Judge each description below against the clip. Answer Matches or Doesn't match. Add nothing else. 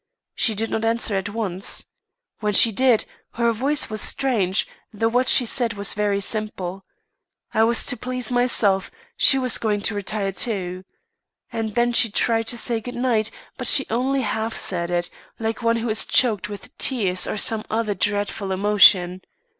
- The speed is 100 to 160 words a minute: Doesn't match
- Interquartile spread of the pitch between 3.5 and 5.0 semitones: Doesn't match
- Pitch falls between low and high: Doesn't match